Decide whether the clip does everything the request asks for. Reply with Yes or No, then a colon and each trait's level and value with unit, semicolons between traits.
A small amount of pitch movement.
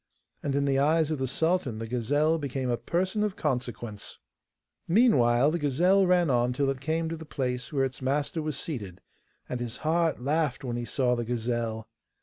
No: average, 4.7 semitones